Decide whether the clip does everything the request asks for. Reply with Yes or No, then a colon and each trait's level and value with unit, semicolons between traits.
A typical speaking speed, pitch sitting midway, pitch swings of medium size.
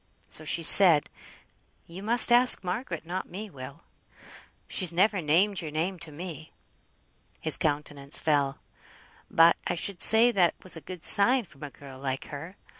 Yes: average, 160 wpm; medium, 170 Hz; average, 4.4 semitones